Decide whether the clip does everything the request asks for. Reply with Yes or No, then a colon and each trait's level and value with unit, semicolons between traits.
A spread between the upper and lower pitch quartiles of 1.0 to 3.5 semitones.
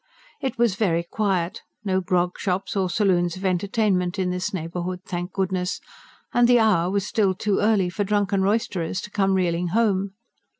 Yes: narrow, 2.4 semitones